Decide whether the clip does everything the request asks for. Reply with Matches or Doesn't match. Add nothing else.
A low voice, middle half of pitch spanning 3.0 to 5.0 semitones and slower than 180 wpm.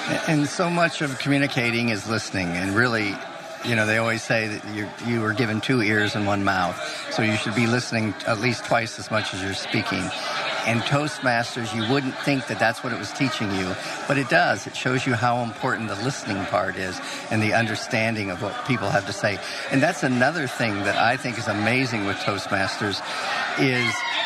Doesn't match